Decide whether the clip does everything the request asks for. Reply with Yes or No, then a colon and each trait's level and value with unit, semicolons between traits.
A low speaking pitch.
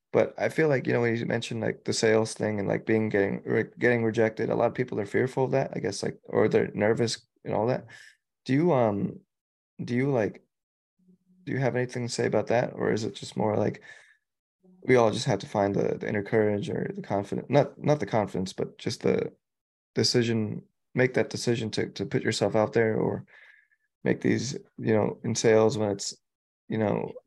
Yes: low, 115 Hz